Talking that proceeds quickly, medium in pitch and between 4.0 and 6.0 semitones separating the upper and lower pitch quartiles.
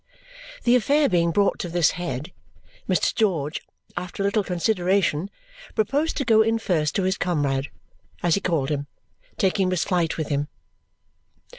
No: average, 155 wpm; medium, 180 Hz; average, 4.5 semitones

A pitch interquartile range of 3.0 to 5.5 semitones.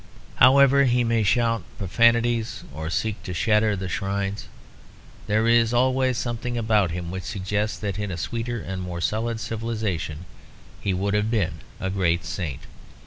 Yes: average, 3.9 semitones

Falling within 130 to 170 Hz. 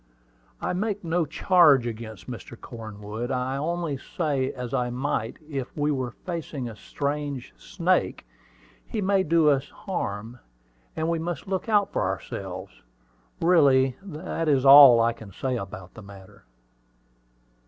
Yes: low, 135 Hz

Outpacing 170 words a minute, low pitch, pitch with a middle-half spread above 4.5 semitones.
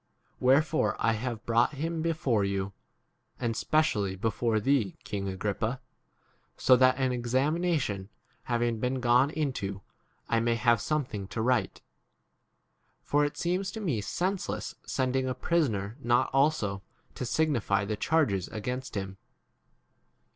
No: slow, 135 wpm; low, 120 Hz; average, 5.2 semitones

